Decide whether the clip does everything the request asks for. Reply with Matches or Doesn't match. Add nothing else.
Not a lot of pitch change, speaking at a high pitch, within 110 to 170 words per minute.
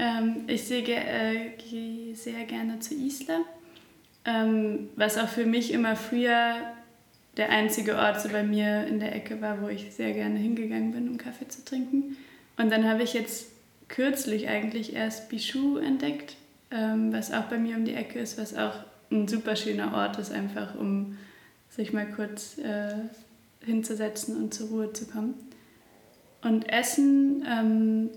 Matches